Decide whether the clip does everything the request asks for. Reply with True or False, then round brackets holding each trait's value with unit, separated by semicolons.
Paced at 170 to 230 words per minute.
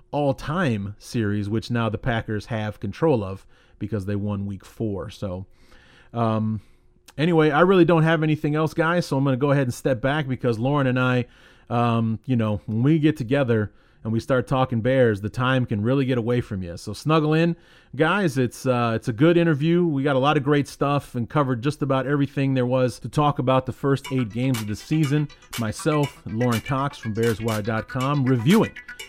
True (200 wpm)